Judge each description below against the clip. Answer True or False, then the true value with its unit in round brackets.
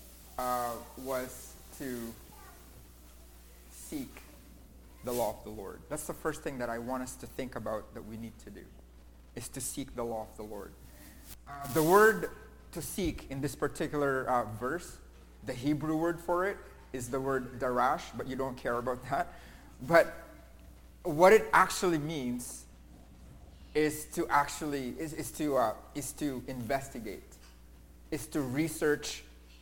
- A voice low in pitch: True (125 Hz)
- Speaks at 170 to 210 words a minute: False (155 wpm)